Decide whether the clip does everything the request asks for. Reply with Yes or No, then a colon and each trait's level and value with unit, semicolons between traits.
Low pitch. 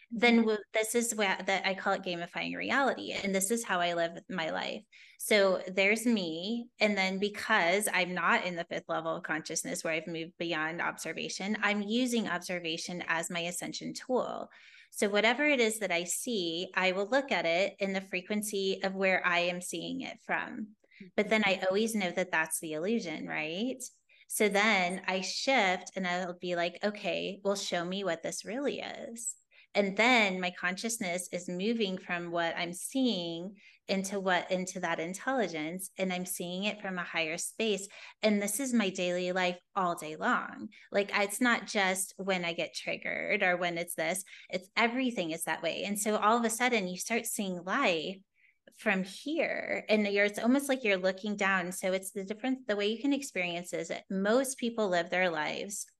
No: high, 195 Hz